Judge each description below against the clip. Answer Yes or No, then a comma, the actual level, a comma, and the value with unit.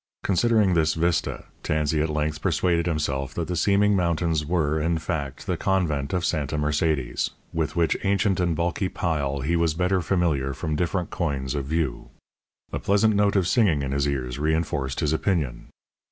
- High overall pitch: No, very low, 80 Hz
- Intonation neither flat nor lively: Yes, average, 3.5 semitones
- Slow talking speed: No, average, 170 wpm